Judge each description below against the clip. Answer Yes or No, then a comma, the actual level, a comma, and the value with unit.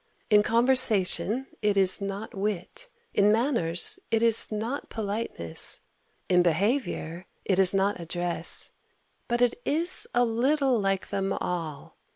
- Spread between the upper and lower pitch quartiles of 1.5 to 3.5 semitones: No, average, 4.4 semitones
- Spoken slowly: Yes, slow, 130 wpm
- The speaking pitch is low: No, high, 210 Hz